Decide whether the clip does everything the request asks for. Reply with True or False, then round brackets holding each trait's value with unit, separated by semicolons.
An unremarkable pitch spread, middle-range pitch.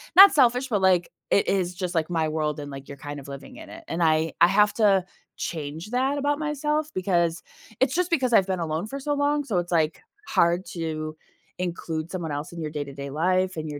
False (6.9 semitones; 175 Hz)